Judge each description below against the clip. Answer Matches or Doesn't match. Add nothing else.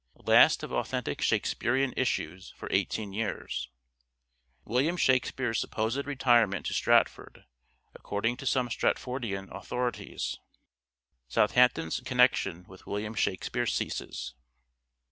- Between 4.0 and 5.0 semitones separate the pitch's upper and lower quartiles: Matches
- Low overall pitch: Matches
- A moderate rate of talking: Doesn't match